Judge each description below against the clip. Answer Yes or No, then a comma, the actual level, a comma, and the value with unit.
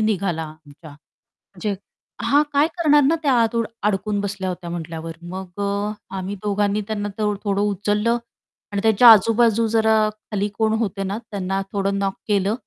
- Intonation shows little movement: Yes, narrow, 2.3 semitones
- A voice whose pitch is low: No, high, 205 Hz